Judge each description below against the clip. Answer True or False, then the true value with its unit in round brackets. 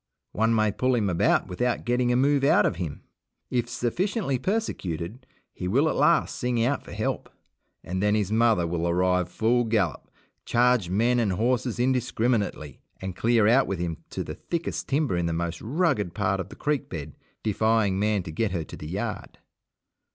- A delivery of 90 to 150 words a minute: False (185 wpm)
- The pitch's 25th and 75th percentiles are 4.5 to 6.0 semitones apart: True (5.3 semitones)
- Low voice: True (110 Hz)